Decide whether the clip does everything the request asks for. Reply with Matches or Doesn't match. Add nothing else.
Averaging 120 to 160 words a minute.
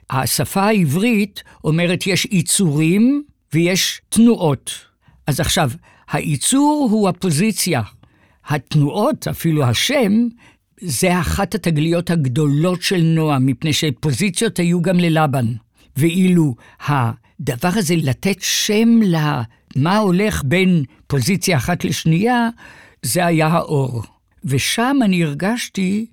Doesn't match